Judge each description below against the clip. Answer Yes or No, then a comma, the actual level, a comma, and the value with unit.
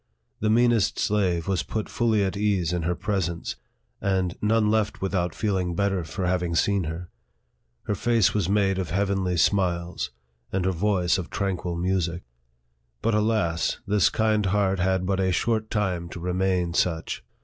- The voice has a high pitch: No, very low, 95 Hz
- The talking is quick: No, average, 165 wpm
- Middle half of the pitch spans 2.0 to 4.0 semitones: Yes, average, 2.8 semitones